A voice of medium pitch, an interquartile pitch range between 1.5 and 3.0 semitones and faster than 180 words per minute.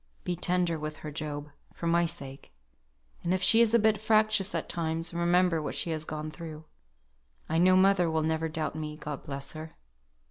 Yes: medium, 165 Hz; average, 2.7 semitones; average, 190 wpm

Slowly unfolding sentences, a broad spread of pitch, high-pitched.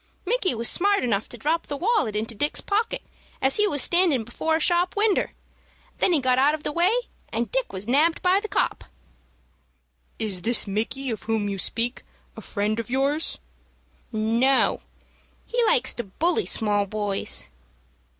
No: average, 170 wpm; wide, 7.9 semitones; very high, 265 Hz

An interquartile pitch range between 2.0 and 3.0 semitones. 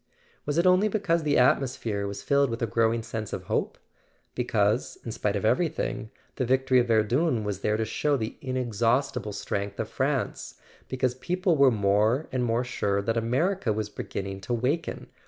No: average, 4.3 semitones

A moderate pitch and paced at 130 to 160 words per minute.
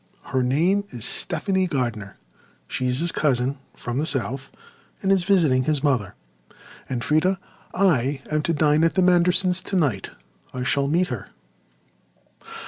Yes: medium, 150 Hz; average, 145 wpm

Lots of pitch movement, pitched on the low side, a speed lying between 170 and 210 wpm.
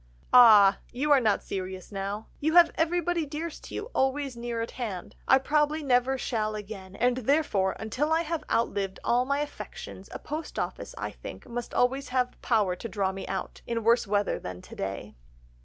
No: wide, 6.1 semitones; high, 240 Hz; average, 190 wpm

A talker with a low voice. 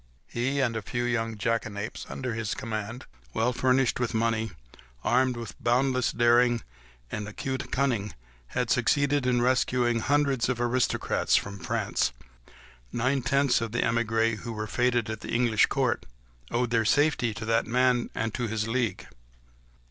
Yes: low, 120 Hz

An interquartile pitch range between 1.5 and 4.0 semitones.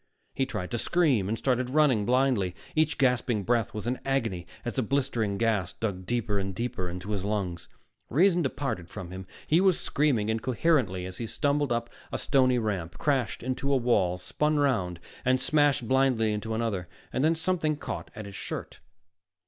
No: wide, 5.4 semitones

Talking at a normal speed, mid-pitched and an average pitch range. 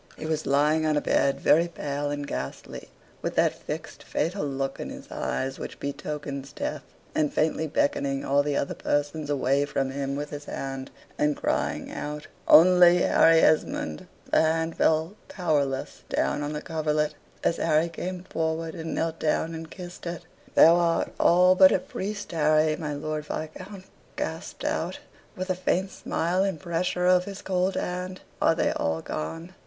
Yes: average, 170 wpm; medium, 155 Hz; average, 3.3 semitones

